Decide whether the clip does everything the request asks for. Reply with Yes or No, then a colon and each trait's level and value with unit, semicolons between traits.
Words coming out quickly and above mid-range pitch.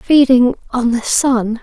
No: average, 150 wpm; high, 245 Hz